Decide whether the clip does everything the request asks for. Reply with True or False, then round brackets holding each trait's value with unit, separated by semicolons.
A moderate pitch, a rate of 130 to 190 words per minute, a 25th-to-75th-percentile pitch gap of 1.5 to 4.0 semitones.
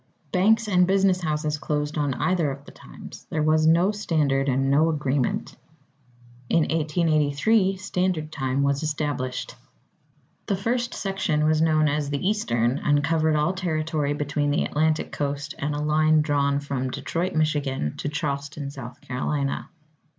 True (150 Hz; 150 wpm; 2.5 semitones)